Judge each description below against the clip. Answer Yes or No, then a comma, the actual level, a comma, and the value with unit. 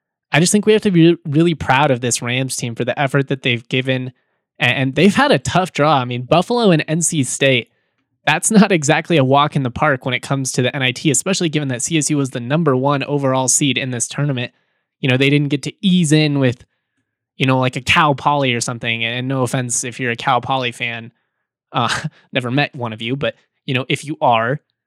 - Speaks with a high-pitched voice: No, low, 135 Hz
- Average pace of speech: No, fast, 230 wpm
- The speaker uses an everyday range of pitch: Yes, average, 3.3 semitones